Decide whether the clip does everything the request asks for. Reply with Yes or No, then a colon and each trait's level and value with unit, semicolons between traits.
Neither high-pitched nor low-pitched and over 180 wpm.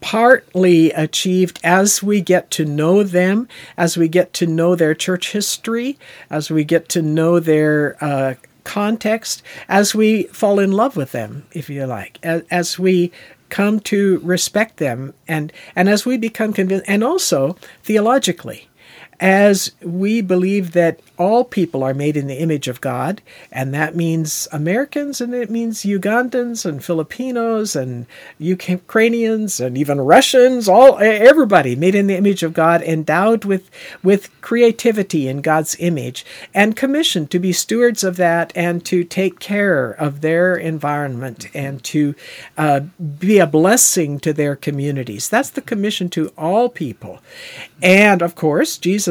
No: medium, 180 Hz; average, 155 wpm